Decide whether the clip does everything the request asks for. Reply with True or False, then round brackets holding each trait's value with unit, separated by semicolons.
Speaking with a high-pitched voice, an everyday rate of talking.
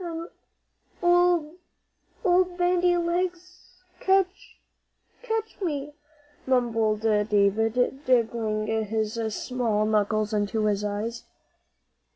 False (250 Hz; 85 wpm)